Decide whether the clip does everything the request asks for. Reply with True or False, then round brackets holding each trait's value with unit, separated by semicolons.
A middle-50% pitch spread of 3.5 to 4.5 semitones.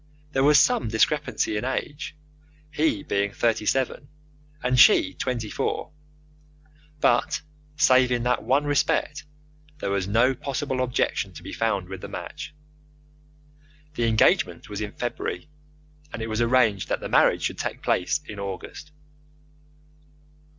True (4.1 semitones)